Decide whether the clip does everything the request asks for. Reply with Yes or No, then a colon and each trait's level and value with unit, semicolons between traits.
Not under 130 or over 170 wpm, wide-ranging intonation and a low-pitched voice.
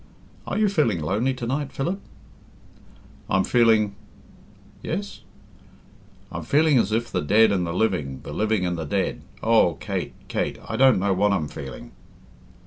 Yes: average, 160 wpm; wide, 6.4 semitones; low, 110 Hz